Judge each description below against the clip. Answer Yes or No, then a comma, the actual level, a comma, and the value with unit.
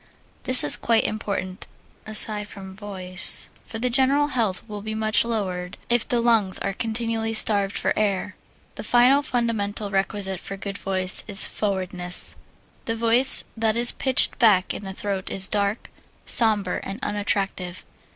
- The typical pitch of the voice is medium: No, high, 210 Hz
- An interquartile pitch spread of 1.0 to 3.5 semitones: Yes, average, 2.8 semitones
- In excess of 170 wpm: No, average, 155 wpm